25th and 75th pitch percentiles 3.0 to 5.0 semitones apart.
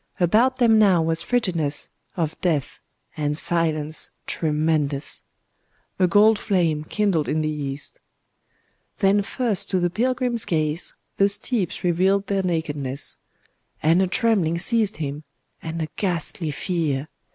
Yes: average, 4.6 semitones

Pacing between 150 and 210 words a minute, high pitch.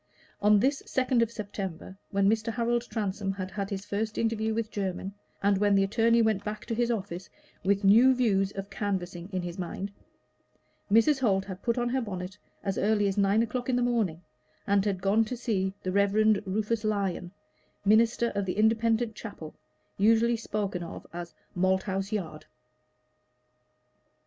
Yes: average, 170 wpm; high, 205 Hz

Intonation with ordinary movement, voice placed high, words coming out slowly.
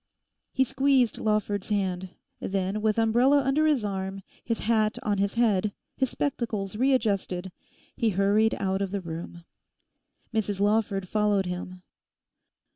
Yes: average, 3.0 semitones; high, 210 Hz; slow, 130 wpm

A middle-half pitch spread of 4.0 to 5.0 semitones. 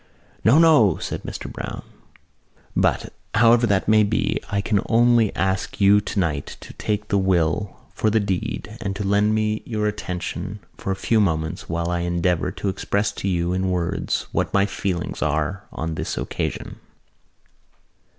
No: average, 3.3 semitones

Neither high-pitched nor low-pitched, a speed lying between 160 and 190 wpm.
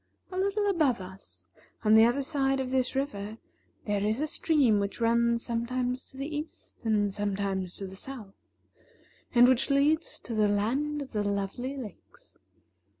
No: high, 240 Hz; average, 165 wpm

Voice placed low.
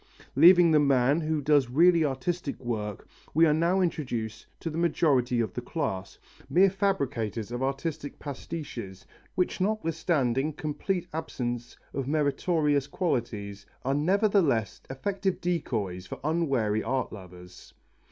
No: medium, 145 Hz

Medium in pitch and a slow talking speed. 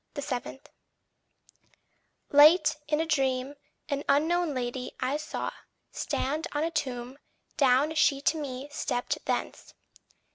No: very high, 285 Hz; slow, 115 wpm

